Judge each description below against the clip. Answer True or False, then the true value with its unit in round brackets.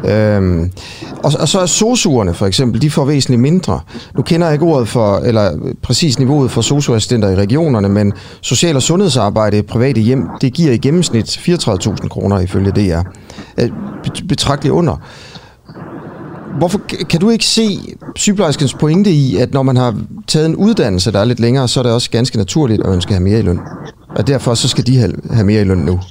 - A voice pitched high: False (125 Hz)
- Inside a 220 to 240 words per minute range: False (190 wpm)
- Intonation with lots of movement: True (6.9 semitones)